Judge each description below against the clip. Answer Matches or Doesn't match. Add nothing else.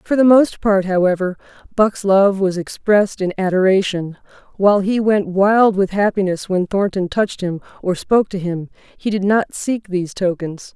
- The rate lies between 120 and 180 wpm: Matches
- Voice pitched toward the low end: Doesn't match